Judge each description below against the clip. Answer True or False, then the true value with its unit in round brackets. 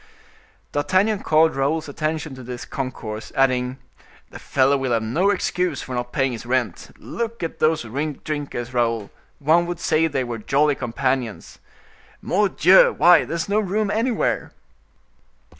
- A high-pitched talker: False (145 Hz)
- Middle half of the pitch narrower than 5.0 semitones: False (5.4 semitones)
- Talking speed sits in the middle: True (145 wpm)